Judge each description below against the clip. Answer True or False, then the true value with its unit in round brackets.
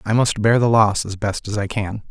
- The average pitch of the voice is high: False (105 Hz)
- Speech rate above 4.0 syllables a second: True (5.1 syllables/s)